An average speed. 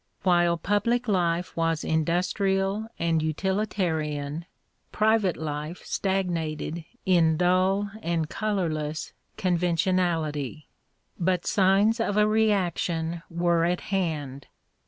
No: slow, 95 wpm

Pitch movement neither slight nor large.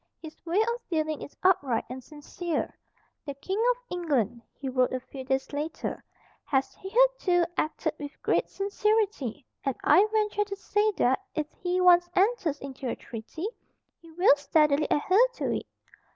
No: wide, 6.2 semitones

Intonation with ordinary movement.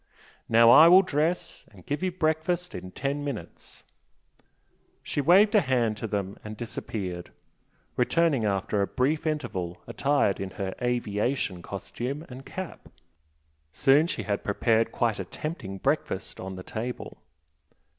No: wide, 7.1 semitones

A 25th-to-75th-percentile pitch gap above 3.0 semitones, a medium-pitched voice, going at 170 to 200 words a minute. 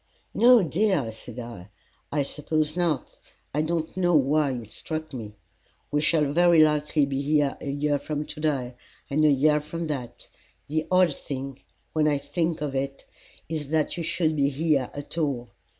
No: narrow, 2.4 semitones; medium, 150 Hz; average, 175 wpm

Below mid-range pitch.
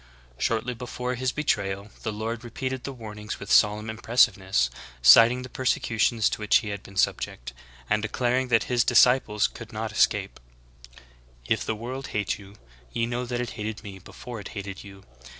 Yes: low, 110 Hz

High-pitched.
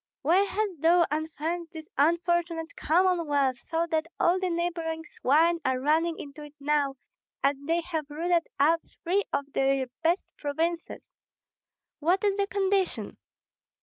Yes: very high, 330 Hz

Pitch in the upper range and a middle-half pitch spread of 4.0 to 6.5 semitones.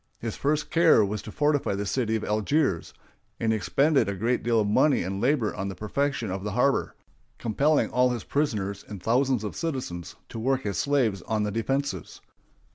No: low, 115 Hz; average, 5.2 semitones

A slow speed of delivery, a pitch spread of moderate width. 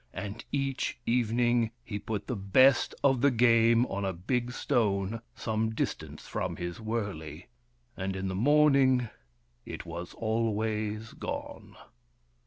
Yes: slow, 130 wpm; average, 3.6 semitones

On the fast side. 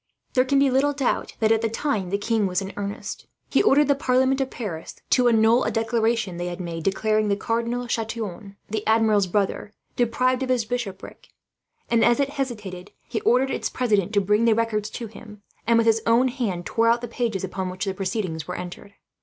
Yes: fast, 210 wpm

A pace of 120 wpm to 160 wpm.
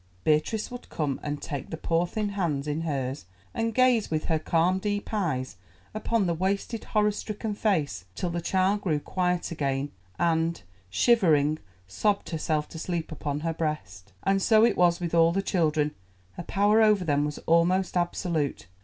No: average, 170 wpm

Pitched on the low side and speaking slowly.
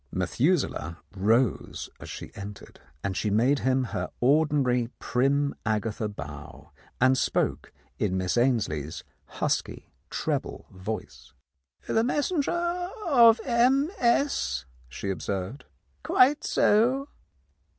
Yes: low, 130 Hz; slow, 110 wpm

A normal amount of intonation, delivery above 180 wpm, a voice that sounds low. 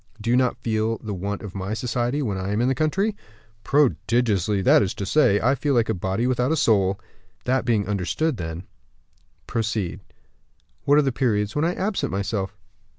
Yes: average, 4.6 semitones; average, 190 wpm; low, 115 Hz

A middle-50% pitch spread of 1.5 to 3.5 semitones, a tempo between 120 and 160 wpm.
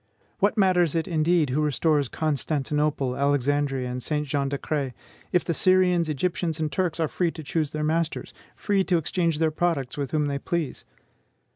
No: average, 3.1 semitones; average, 170 wpm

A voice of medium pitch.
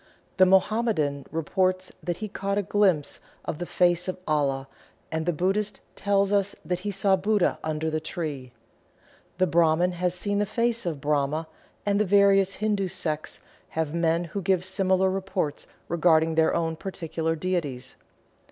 Yes: medium, 180 Hz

